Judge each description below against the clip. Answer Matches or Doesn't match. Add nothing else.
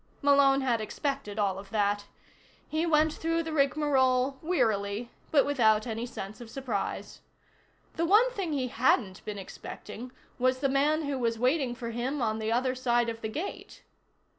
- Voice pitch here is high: Matches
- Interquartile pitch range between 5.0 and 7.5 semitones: Doesn't match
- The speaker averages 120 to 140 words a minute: Doesn't match